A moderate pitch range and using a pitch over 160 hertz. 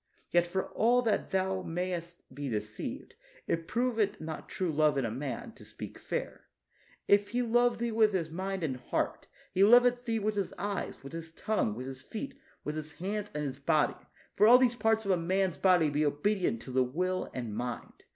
No: wide, 6.3 semitones; medium, 185 Hz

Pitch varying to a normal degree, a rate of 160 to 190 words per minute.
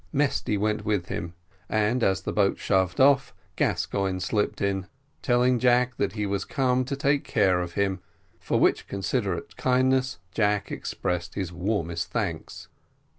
No: average, 4.9 semitones; average, 150 wpm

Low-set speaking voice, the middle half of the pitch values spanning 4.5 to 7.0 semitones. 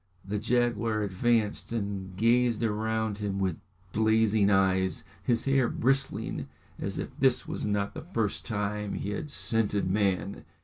No: low, 105 Hz; narrow, 2.5 semitones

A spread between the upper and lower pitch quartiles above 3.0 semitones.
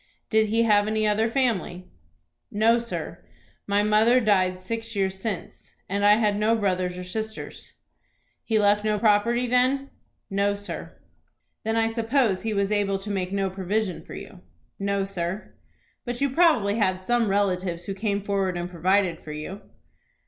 No: average, 2.7 semitones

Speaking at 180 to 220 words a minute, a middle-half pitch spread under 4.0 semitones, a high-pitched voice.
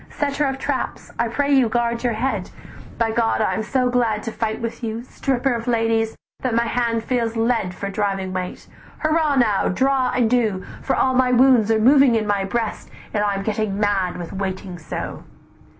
Yes: average, 195 wpm; average, 3.1 semitones; high, 230 Hz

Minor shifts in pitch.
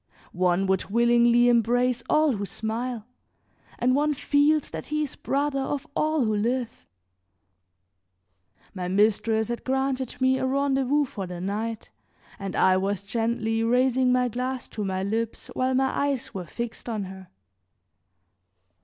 No: average, 3.8 semitones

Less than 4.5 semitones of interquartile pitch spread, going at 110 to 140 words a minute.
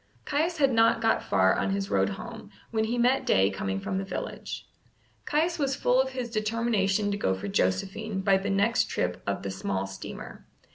No: average, 3.9 semitones; average, 195 wpm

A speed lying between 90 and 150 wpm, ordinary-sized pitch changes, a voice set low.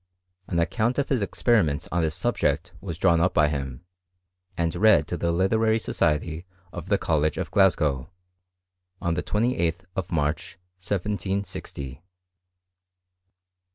Yes: slow, 135 wpm; average, 4.2 semitones; very low, 85 Hz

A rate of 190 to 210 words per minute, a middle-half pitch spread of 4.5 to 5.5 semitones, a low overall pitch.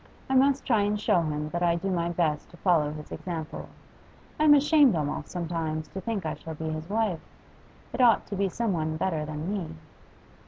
No: average, 200 wpm; average, 4.8 semitones; medium, 175 Hz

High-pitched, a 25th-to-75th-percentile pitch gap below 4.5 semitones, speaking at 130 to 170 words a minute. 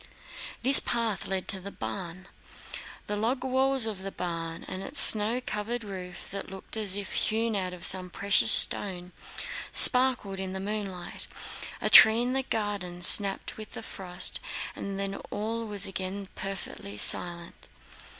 Yes: high, 200 Hz; average, 2.9 semitones; average, 155 wpm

